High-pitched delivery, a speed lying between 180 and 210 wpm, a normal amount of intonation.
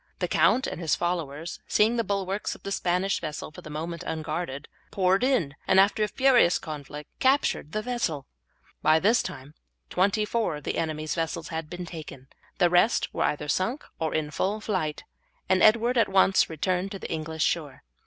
No: medium, 175 Hz; average, 185 wpm; average, 4.7 semitones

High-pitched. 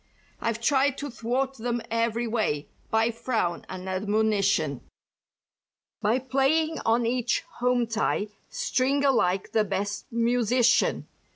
Yes: high, 230 Hz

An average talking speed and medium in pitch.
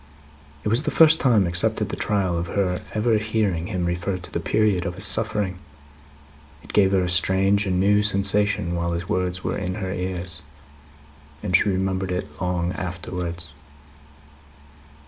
No: average, 165 wpm; very low, 95 Hz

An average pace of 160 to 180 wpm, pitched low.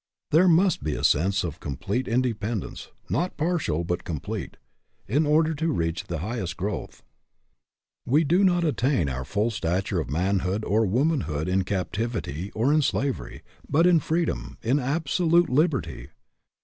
No: average, 150 wpm; low, 115 Hz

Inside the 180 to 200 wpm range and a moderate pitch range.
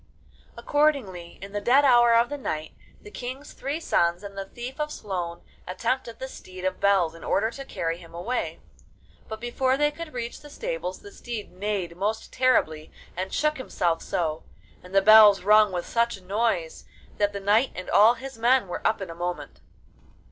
No: average, 185 wpm; wide, 5.9 semitones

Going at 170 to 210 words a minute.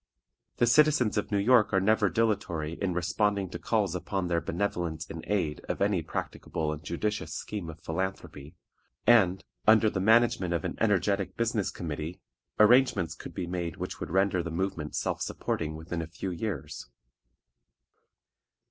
No: average, 155 wpm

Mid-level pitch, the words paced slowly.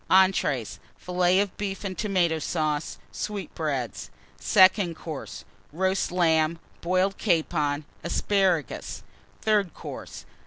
Yes: medium, 175 Hz; slow, 95 wpm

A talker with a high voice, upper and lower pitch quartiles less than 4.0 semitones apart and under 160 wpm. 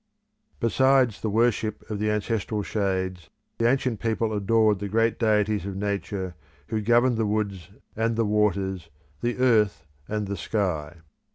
No: low, 105 Hz; narrow, 2.4 semitones; average, 150 wpm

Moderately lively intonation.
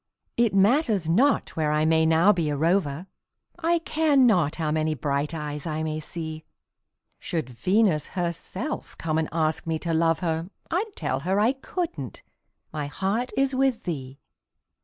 No: wide, 6.0 semitones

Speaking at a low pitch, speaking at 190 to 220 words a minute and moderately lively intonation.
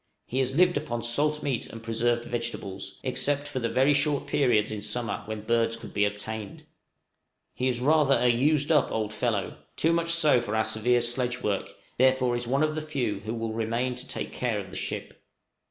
Yes: low, 120 Hz; average, 200 wpm; average, 4.0 semitones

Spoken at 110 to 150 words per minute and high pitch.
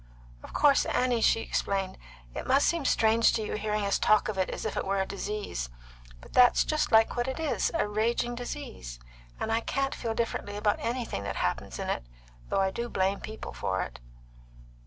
No: average, 200 wpm; high, 220 Hz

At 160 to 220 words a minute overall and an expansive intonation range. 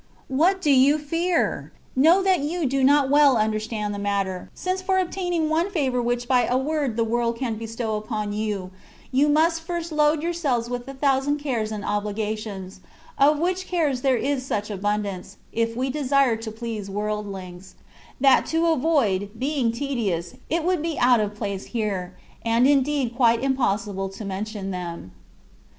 Yes: average, 170 wpm; wide, 5.8 semitones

